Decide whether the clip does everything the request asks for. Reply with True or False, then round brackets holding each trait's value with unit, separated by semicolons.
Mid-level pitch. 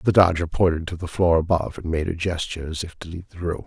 False (85 Hz)